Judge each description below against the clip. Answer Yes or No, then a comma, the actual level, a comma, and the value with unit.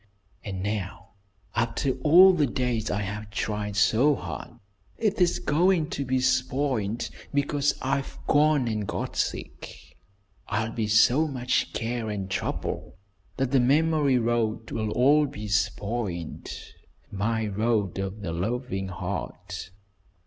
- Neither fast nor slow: No, slow, 130 wpm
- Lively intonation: No, average, 4.9 semitones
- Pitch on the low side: Yes, low, 115 Hz